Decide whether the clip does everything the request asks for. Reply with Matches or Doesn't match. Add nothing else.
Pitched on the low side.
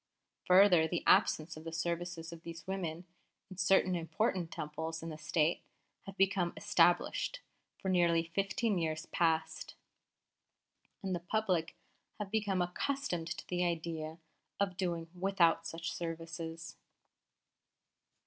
Doesn't match